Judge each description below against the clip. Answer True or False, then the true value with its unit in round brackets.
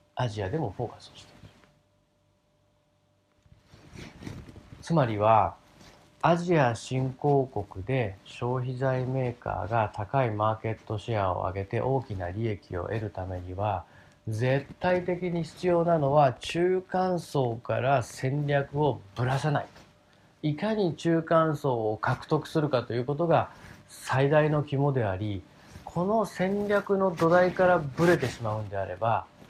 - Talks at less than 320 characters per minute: True (260 characters per minute)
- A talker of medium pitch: False (130 Hz)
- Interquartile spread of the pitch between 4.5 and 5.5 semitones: False (6.6 semitones)